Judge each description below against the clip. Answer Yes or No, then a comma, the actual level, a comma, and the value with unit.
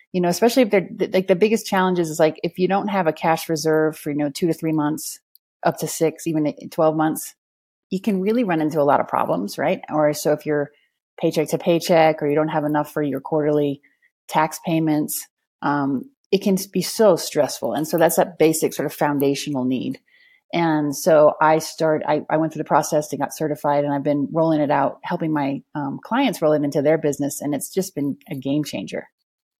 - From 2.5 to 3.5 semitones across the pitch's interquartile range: Yes, average, 2.8 semitones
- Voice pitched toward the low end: No, medium, 155 Hz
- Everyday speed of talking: No, fast, 220 wpm